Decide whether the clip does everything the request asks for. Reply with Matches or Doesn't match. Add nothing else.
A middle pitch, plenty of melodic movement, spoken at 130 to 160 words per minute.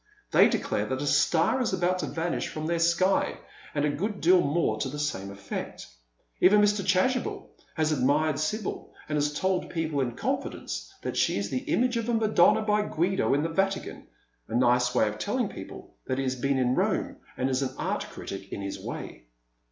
Doesn't match